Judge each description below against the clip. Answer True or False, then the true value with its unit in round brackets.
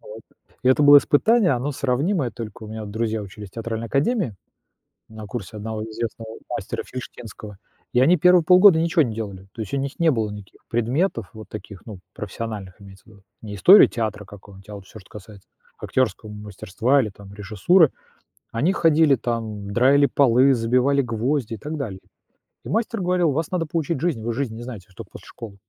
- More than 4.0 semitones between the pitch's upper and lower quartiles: True (5.2 semitones)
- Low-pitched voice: True (115 Hz)